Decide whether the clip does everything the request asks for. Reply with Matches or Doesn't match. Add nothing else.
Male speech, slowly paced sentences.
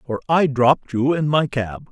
Doesn't match